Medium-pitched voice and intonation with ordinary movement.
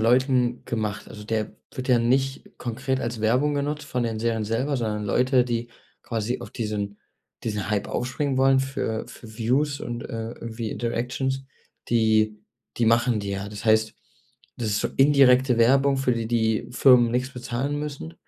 No: low, 120 Hz; average, 3.1 semitones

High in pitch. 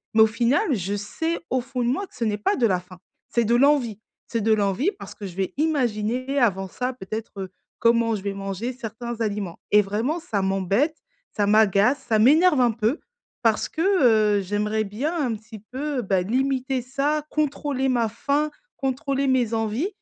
Yes: high, 235 Hz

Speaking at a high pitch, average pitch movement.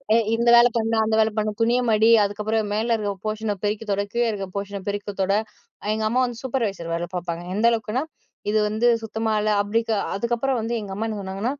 No: high, 215 Hz; narrow, 2.0 semitones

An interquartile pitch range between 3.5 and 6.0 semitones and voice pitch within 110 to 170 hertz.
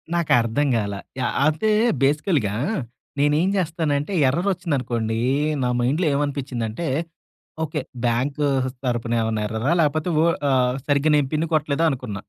Yes: average, 4.6 semitones; medium, 140 Hz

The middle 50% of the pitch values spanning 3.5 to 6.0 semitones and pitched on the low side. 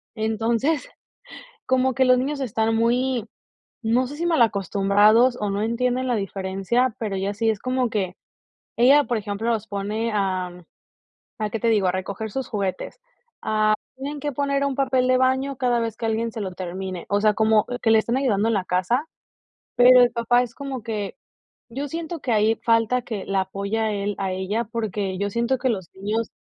No: average, 3.9 semitones; high, 225 Hz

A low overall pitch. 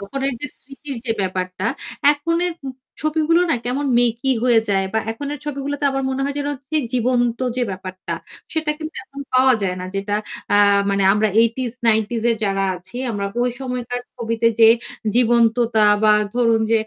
No: high, 240 Hz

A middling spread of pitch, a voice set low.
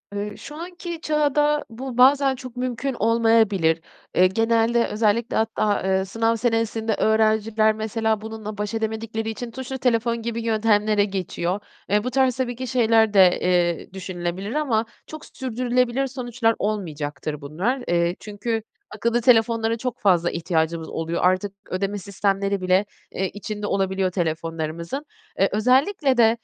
No: average, 3.8 semitones; high, 220 Hz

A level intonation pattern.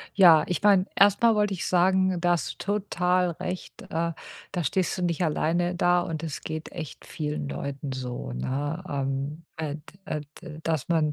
No: average, 3.4 semitones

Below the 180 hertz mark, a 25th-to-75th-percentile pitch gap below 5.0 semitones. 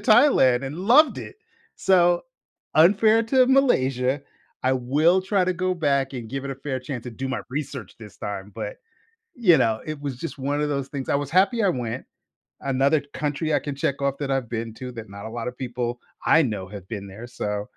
No: low, 135 Hz; wide, 5.6 semitones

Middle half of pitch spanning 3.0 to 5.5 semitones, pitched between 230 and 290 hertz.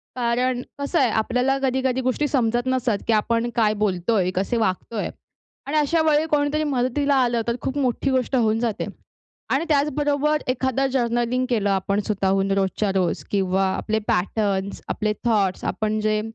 Yes: average, 4.1 semitones; high, 240 Hz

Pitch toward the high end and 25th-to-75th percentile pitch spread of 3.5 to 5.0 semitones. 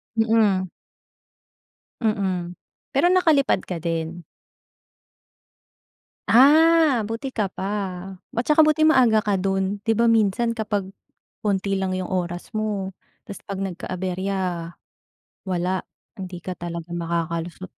Yes: high, 195 Hz; average, 3.9 semitones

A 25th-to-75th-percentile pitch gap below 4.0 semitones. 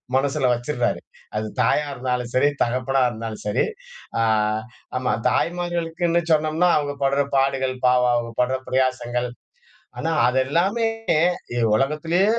No: average, 4.3 semitones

